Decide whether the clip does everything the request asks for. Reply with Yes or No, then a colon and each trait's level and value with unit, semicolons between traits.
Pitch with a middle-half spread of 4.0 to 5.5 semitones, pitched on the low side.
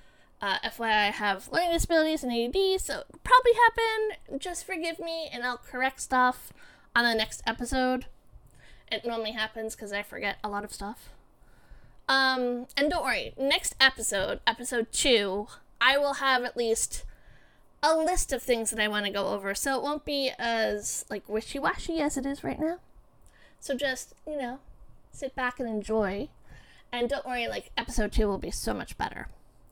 No: average, 4.4 semitones; very high, 250 Hz